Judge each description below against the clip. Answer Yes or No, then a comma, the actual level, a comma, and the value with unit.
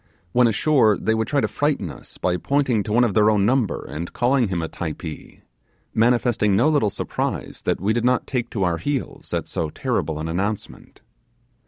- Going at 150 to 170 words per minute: No, average, 195 wpm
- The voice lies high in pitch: No, low, 110 Hz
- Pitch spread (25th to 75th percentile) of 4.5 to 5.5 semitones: Yes, average, 5.0 semitones